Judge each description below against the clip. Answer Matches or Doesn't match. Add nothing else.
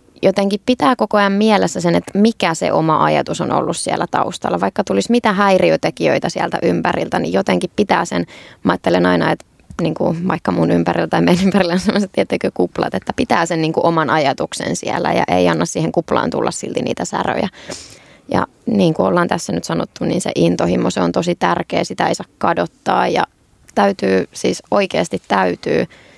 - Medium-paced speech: Doesn't match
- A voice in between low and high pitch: Matches